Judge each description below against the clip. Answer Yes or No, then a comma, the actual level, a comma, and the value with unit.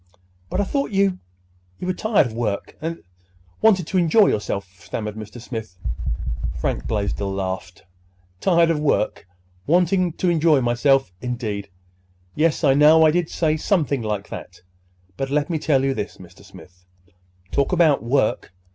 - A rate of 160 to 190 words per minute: No, average, 145 wpm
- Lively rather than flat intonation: Yes, wide, 8.9 semitones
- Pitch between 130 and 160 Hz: Yes, low, 135 Hz